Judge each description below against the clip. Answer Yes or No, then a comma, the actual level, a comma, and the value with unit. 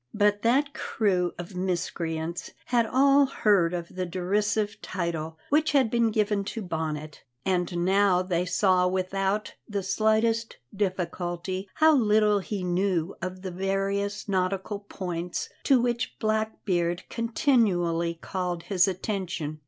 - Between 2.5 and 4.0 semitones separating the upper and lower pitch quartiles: Yes, average, 3.3 semitones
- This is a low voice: No, high, 190 Hz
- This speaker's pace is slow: Yes, slow, 130 wpm